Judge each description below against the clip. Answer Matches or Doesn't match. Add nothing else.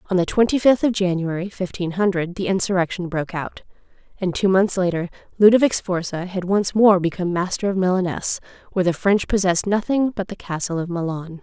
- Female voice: Matches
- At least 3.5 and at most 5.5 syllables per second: Doesn't match